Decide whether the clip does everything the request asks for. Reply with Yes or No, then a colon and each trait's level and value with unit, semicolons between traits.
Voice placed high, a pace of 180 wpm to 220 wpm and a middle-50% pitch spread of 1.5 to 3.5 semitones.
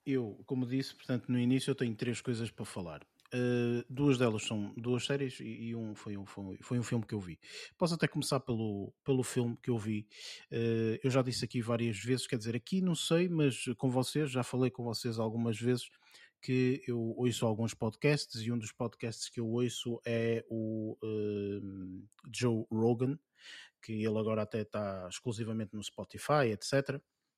No: low, 120 Hz; fast, 185 wpm; average, 2.7 semitones